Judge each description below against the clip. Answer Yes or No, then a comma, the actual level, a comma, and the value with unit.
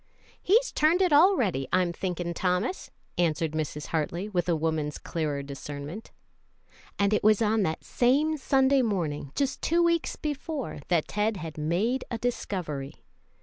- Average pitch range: No, wide, 8.8 semitones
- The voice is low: No, high, 190 Hz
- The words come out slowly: No, average, 145 wpm